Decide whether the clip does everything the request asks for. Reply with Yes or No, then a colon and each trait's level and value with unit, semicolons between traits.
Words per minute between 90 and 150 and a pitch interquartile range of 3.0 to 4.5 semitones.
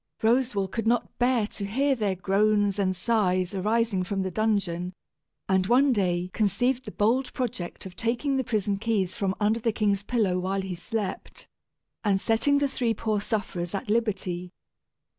No: average, 165 wpm; average, 3.5 semitones